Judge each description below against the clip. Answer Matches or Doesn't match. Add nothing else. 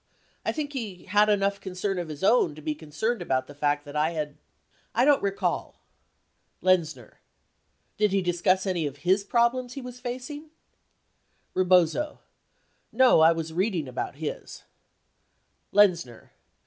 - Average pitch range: Doesn't match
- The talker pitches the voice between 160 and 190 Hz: Matches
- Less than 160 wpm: Matches